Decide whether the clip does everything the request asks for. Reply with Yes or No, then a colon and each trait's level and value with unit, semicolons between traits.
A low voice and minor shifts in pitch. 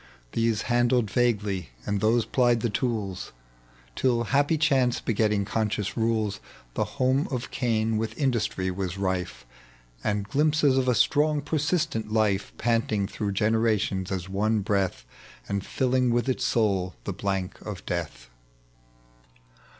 No: low, 110 Hz; average, 3.8 semitones